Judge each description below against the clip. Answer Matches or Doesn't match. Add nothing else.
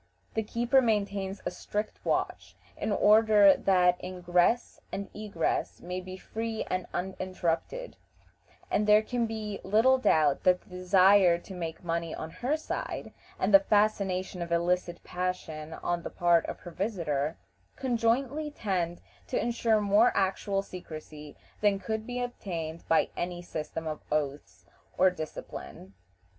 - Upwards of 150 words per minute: Doesn't match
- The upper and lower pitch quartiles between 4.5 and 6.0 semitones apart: Doesn't match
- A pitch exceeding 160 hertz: Matches